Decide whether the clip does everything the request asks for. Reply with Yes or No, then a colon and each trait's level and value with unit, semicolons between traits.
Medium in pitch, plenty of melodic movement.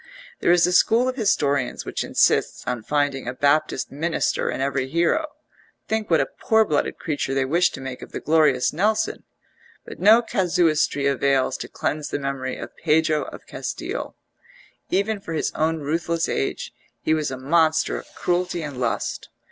No: medium, 155 Hz; average, 4.3 semitones